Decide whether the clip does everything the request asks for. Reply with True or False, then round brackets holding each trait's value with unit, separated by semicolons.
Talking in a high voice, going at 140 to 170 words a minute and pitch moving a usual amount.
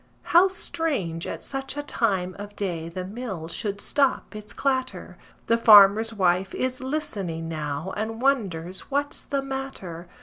False (210 Hz; 145 wpm; 6.8 semitones)